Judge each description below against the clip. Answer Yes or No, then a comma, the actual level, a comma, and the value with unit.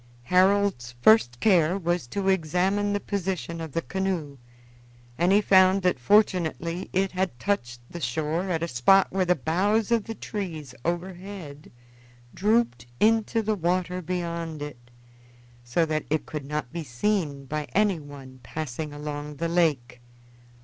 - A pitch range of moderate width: Yes, average, 4.6 semitones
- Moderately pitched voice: Yes, medium, 170 Hz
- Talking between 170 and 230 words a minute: No, average, 145 wpm